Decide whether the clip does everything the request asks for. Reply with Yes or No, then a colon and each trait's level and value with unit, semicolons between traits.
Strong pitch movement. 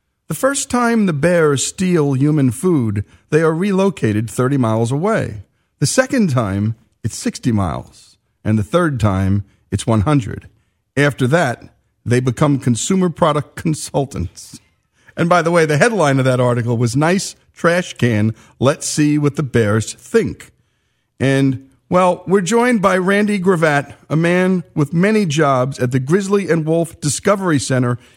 Yes: wide, 7.1 semitones